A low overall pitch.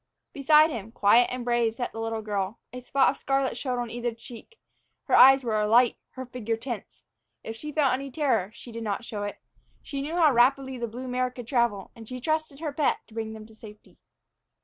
No: high, 245 Hz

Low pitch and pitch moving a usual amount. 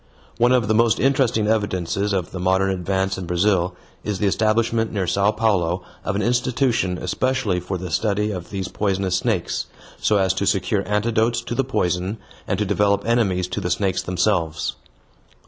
Yes: low, 100 Hz; average, 3.1 semitones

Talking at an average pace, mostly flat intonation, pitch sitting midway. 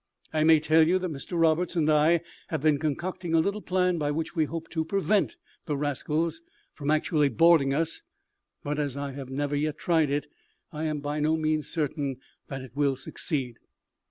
Yes: average, 190 wpm; narrow, 2.3 semitones; medium, 155 Hz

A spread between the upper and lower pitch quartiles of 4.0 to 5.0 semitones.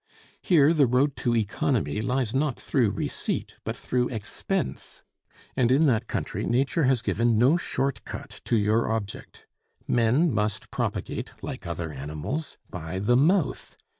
Yes: average, 4.3 semitones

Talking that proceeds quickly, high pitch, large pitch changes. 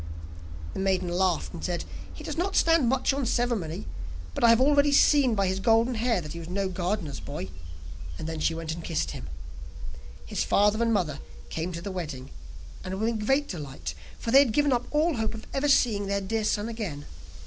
Yes: fast, 210 wpm; high, 205 Hz; wide, 5.9 semitones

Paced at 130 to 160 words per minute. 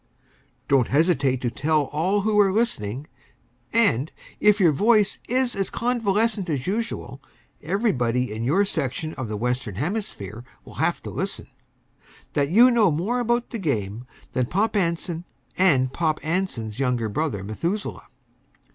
Yes: average, 145 wpm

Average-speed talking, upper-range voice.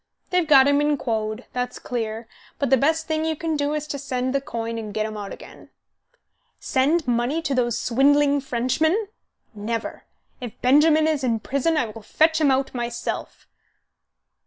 Yes: average, 175 wpm; very high, 270 Hz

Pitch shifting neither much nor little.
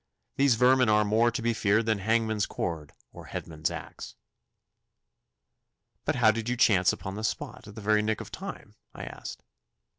No: narrow, 2.1 semitones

